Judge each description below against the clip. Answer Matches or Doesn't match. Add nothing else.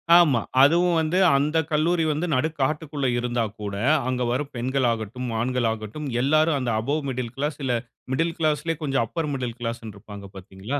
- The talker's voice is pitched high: Doesn't match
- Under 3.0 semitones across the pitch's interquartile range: Doesn't match